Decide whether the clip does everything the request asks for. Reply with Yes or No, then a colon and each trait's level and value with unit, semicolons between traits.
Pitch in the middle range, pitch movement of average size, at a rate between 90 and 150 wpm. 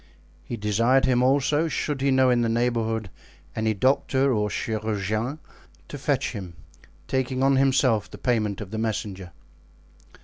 No: low, 120 Hz; average, 3.6 semitones; average, 145 wpm